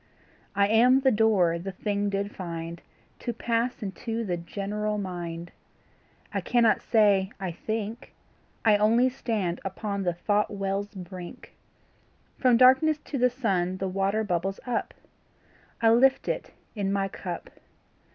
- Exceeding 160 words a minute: No, average, 140 wpm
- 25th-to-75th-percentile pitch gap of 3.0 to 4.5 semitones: Yes, average, 3.4 semitones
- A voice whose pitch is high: Yes, high, 205 Hz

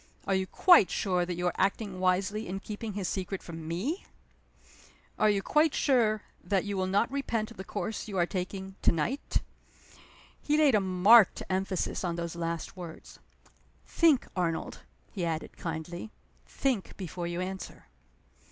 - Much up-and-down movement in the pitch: No, average, 3.4 semitones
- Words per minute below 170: Yes, average, 160 wpm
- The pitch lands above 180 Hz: Yes, high, 190 Hz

